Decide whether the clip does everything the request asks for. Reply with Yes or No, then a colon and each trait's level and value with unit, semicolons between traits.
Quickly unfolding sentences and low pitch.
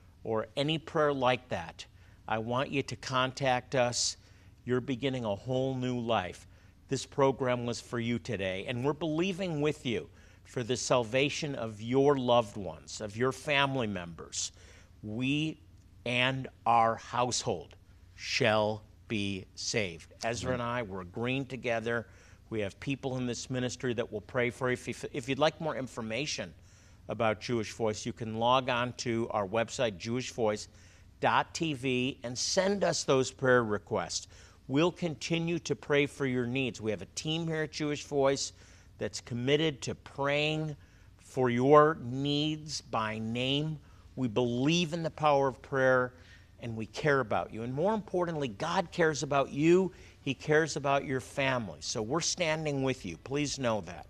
No: average, 155 wpm; low, 125 Hz